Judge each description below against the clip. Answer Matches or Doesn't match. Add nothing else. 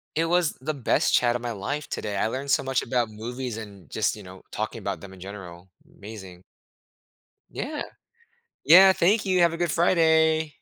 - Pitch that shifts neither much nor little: Doesn't match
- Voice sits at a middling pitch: Doesn't match